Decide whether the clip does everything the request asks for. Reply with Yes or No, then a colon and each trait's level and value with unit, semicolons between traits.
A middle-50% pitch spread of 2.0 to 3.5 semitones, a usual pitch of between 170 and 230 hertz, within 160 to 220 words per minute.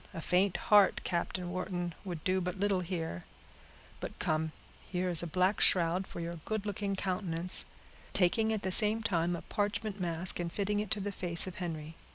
Yes: average, 2.8 semitones; medium, 185 Hz; average, 190 wpm